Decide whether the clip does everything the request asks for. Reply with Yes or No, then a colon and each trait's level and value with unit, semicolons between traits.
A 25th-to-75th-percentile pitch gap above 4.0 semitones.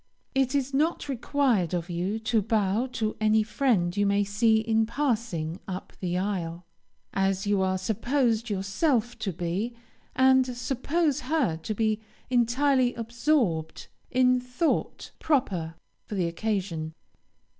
Yes: average, 5.0 semitones